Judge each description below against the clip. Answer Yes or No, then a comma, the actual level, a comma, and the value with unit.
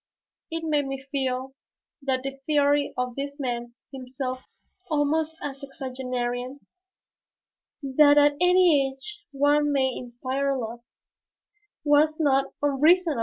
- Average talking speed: No, slow, 115 wpm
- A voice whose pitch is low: No, very high, 275 Hz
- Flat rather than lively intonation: Yes, narrow, 2.2 semitones